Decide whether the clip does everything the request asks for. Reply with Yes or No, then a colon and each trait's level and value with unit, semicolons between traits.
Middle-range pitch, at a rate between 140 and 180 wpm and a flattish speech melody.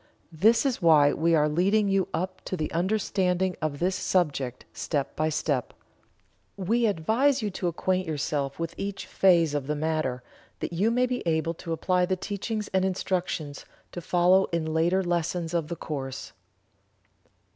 No: medium, 175 Hz; average, 165 wpm; average, 3.4 semitones